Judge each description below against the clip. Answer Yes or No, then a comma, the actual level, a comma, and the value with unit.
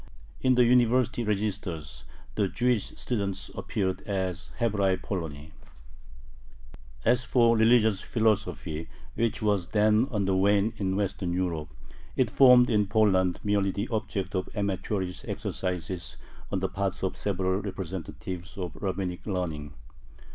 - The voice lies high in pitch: No, low, 100 Hz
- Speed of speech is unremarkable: No, slow, 125 wpm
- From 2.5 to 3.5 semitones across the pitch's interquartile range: Yes, average, 2.9 semitones